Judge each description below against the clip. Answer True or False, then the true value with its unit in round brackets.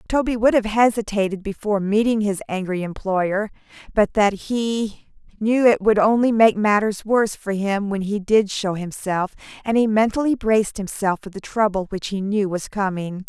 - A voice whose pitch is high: True (210 Hz)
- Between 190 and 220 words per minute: False (175 wpm)